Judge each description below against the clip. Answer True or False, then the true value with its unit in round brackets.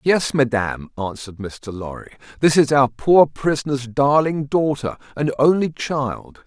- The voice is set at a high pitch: False (135 Hz)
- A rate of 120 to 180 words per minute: True (140 wpm)